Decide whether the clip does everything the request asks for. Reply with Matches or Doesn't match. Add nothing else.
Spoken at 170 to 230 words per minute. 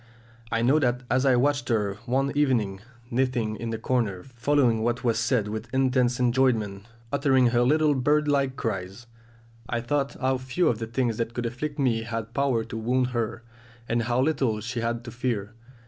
Matches